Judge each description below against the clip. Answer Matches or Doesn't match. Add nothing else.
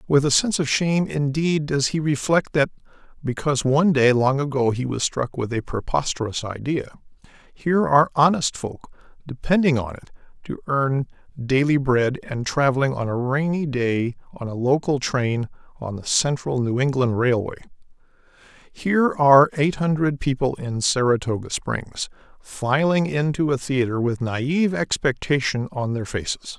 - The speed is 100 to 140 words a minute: Doesn't match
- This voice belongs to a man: Matches